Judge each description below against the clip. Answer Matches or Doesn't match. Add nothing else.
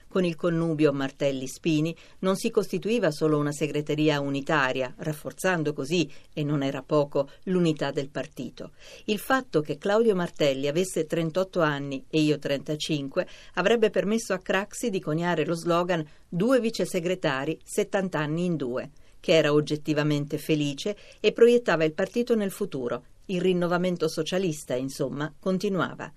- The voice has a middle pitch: Matches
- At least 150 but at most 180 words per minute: Doesn't match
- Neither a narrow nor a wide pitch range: Matches